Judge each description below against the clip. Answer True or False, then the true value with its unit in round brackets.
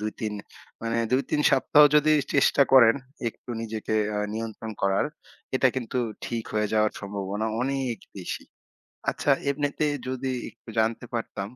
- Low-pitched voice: True (115 Hz)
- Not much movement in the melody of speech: False (3.7 semitones)